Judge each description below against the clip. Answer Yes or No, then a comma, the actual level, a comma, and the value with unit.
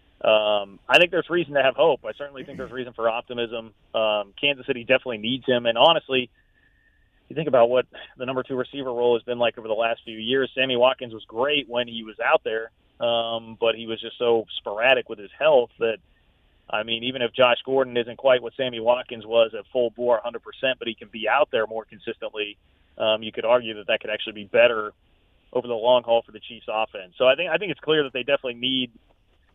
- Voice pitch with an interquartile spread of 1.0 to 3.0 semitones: Yes, narrow, 2.6 semitones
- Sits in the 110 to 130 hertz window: Yes, low, 120 Hz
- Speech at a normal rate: No, fast, 235 wpm